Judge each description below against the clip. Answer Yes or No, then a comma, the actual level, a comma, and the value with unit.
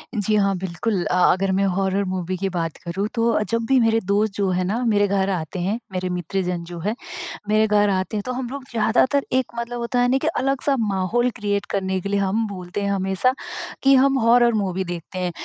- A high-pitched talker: Yes, high, 200 Hz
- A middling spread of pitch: Yes, average, 3.6 semitones